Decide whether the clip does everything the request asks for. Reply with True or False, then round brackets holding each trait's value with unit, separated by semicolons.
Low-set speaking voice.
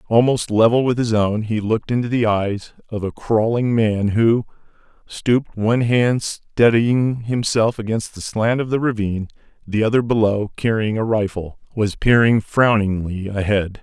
True (110 Hz)